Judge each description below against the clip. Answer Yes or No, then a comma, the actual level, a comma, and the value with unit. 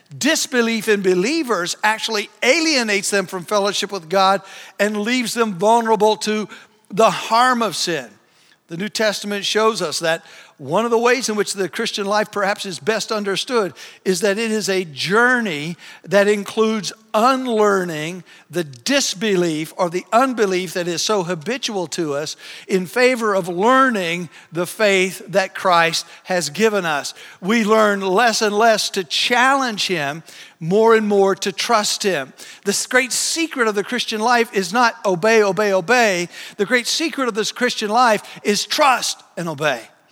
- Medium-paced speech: Yes, average, 160 wpm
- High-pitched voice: Yes, high, 210 Hz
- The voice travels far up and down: No, average, 3.5 semitones